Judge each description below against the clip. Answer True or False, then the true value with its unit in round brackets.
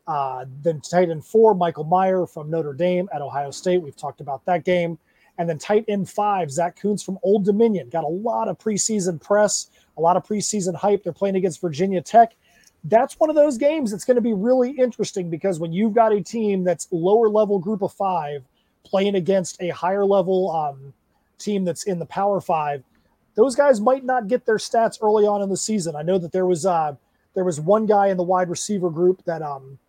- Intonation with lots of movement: False (3.5 semitones)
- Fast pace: True (215 wpm)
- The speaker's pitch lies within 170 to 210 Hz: True (190 Hz)